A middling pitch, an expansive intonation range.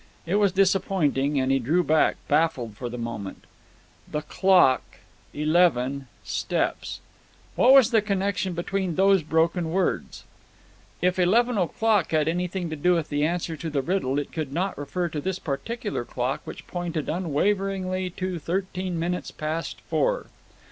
No: medium, 175 Hz; average, 4.2 semitones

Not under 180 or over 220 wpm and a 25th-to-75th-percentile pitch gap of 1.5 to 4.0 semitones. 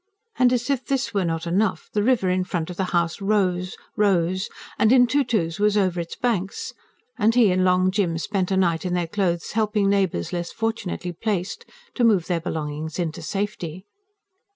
Yes: average, 185 wpm; average, 3.6 semitones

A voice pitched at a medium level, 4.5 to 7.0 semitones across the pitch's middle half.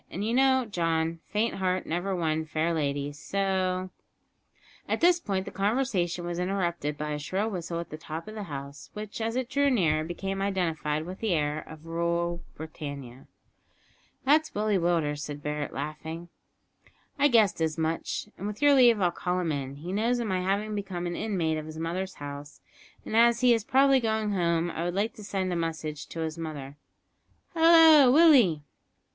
Yes: medium, 175 Hz; average, 5.1 semitones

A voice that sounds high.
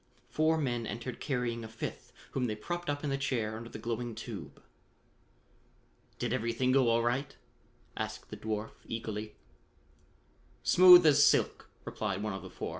No: low, 120 Hz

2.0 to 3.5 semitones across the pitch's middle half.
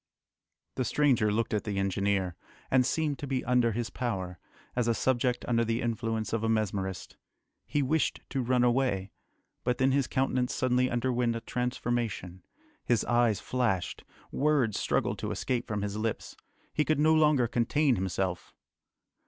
Yes: average, 3.2 semitones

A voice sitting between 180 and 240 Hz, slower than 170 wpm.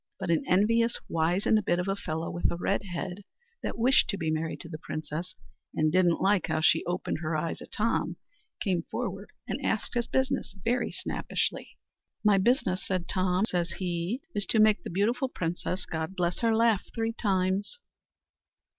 No: medium, 185 Hz; average, 180 wpm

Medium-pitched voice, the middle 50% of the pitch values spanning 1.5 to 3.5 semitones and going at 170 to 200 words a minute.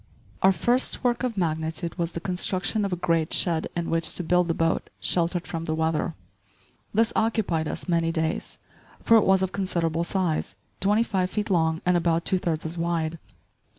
Yes: medium, 170 Hz; average, 2.7 semitones; average, 190 wpm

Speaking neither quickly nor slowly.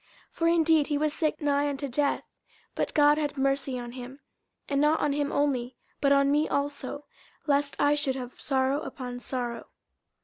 Yes: average, 180 wpm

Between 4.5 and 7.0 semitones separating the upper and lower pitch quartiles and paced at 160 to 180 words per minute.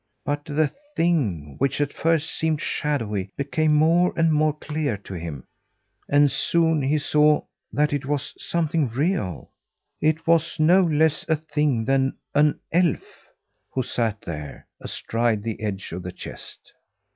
No: wide, 5.4 semitones; average, 145 wpm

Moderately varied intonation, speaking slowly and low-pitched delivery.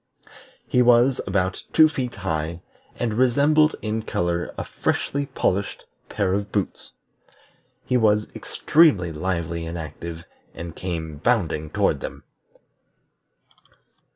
No: wide, 6.5 semitones; slow, 115 wpm; low, 100 Hz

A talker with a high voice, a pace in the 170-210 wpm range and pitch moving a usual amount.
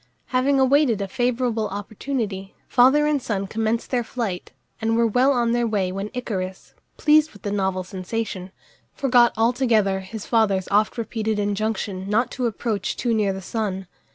No: high, 220 Hz; average, 160 wpm; average, 3.8 semitones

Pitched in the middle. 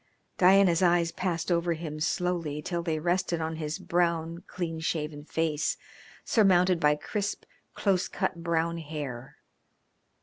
Yes: medium, 170 Hz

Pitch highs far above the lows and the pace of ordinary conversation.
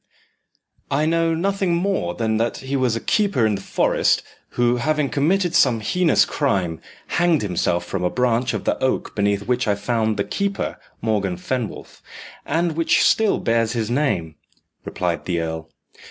Yes: wide, 7.8 semitones; average, 165 wpm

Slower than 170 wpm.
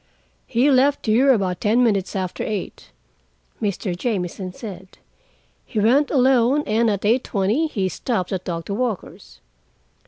Yes: slow, 135 wpm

